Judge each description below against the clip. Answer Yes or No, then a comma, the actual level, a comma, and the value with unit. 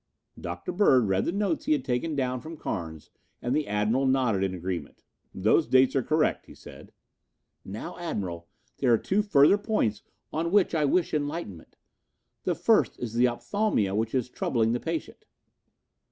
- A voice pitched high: No, low, 130 Hz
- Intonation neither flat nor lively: No, wide, 7.1 semitones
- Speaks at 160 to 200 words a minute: Yes, average, 165 wpm